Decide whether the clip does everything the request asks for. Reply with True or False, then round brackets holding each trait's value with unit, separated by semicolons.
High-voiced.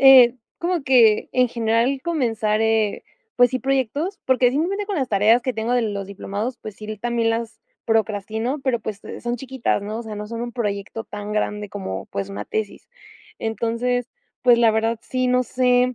True (230 Hz)